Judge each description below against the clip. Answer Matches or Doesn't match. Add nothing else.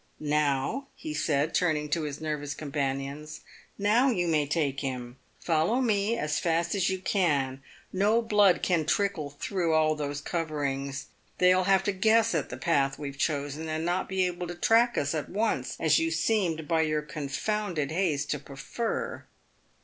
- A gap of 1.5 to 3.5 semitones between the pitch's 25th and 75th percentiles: Doesn't match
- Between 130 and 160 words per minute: Doesn't match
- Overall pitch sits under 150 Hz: Doesn't match